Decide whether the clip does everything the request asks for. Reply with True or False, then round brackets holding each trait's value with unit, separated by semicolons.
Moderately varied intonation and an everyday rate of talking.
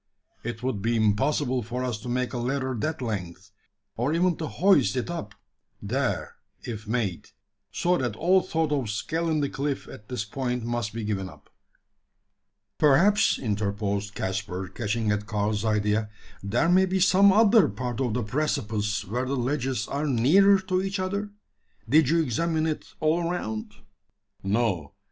False (6.9 semitones; 160 wpm)